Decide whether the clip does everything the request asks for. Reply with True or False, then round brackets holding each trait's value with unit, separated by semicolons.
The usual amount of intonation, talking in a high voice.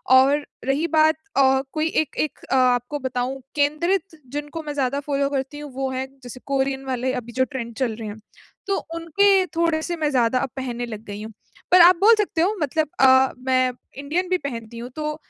True (3.4 semitones; 275 Hz)